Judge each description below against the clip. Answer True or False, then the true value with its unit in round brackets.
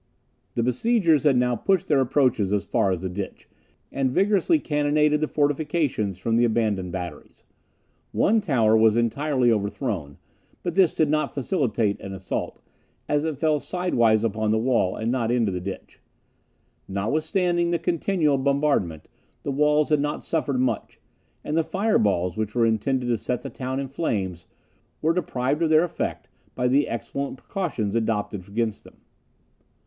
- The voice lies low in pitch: True (130 Hz)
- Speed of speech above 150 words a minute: True (160 wpm)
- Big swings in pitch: True (5.9 semitones)